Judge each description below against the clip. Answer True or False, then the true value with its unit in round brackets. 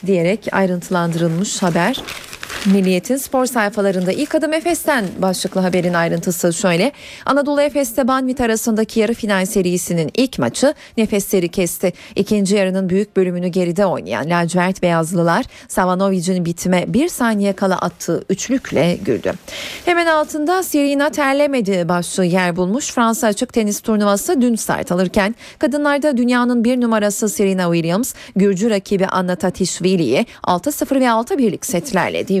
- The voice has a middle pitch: False (200 Hz)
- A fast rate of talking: False (130 wpm)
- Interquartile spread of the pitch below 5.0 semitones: False (5.4 semitones)